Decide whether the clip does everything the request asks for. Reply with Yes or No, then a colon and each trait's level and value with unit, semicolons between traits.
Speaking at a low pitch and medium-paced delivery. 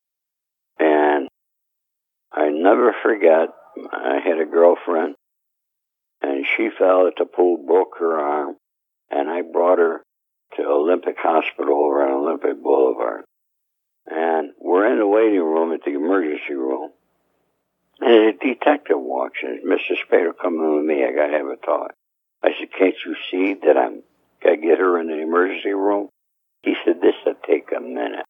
Yes: low, 100 Hz; average, 160 wpm